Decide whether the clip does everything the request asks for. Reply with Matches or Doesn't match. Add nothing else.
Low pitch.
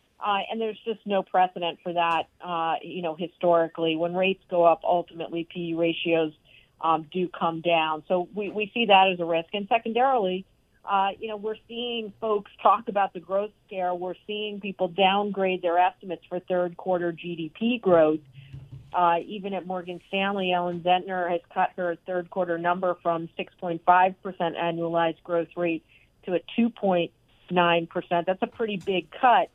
Doesn't match